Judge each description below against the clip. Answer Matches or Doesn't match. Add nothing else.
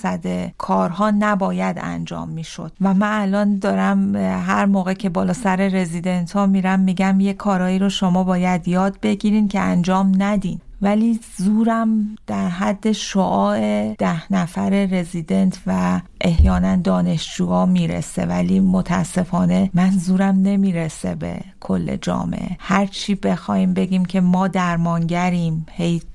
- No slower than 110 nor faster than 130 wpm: Matches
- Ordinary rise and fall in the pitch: Matches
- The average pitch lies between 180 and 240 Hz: Matches